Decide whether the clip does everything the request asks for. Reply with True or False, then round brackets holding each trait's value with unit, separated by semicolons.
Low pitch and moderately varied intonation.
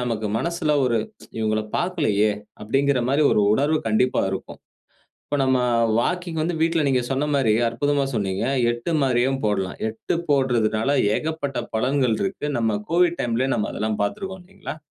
False (130 Hz; 5.7 semitones)